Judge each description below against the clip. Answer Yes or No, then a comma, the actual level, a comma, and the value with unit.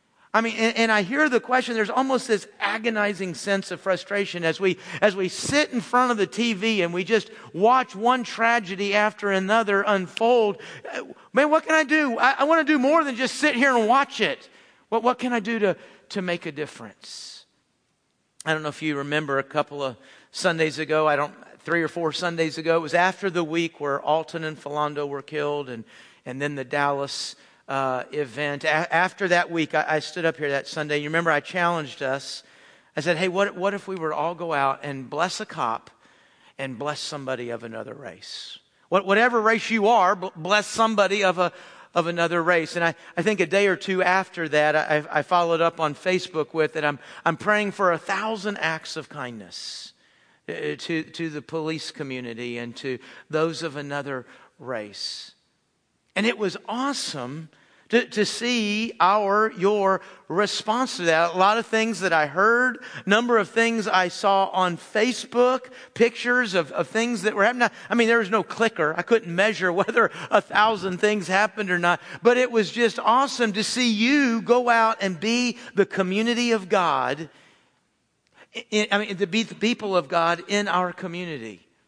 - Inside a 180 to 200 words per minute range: Yes, average, 190 wpm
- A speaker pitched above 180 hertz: Yes, high, 190 Hz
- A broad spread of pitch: Yes, wide, 6.0 semitones